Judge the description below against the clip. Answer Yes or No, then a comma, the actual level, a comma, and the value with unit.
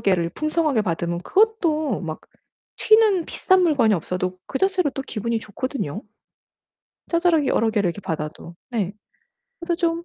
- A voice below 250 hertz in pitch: No, very high, 255 Hz